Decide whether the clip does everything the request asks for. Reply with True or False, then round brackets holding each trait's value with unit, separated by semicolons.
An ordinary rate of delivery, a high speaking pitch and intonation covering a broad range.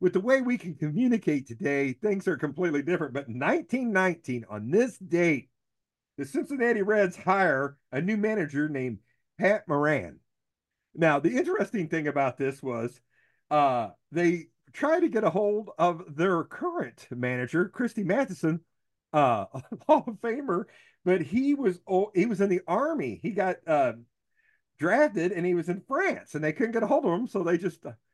False (170 wpm; 180 Hz; 7.6 semitones)